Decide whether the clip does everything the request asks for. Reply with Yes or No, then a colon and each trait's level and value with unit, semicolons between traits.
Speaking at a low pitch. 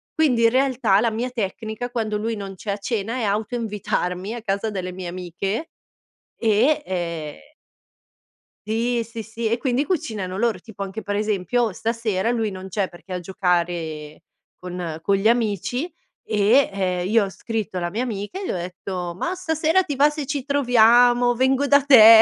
No: high, 220 Hz